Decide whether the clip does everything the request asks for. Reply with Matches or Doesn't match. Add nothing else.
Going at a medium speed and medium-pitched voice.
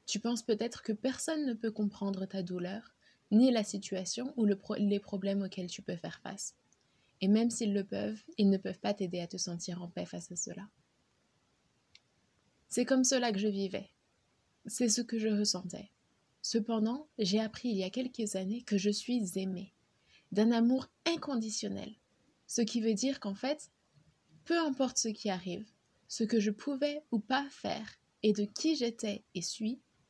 Doesn't match